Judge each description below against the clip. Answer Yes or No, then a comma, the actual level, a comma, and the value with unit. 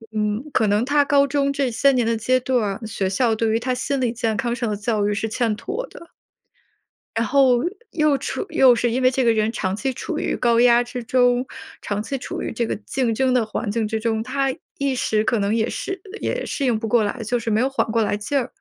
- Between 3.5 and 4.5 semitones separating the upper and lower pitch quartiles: No, average, 3.0 semitones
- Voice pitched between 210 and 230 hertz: No, high, 240 Hz